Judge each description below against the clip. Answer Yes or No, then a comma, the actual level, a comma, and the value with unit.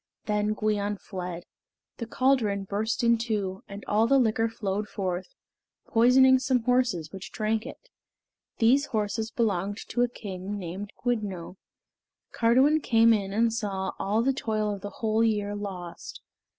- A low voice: No, high, 215 Hz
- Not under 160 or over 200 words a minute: No, average, 150 wpm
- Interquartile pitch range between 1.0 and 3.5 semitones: Yes, average, 2.8 semitones